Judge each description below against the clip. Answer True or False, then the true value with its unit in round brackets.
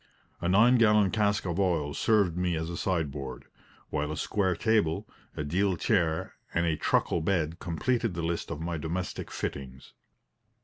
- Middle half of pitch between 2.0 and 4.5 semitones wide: True (3.8 semitones)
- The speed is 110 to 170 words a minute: True (165 wpm)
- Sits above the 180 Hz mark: False (85 Hz)